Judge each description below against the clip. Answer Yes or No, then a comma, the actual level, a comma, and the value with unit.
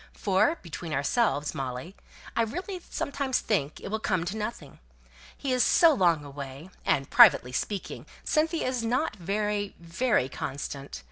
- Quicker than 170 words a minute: No, average, 145 wpm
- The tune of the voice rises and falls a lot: Yes, wide, 8.8 semitones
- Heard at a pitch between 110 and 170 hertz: No, high, 195 Hz